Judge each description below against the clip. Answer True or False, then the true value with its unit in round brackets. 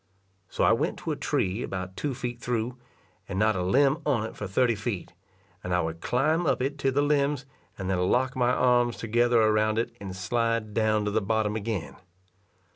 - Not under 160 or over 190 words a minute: False (200 wpm)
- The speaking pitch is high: False (115 Hz)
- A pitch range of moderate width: True (3.8 semitones)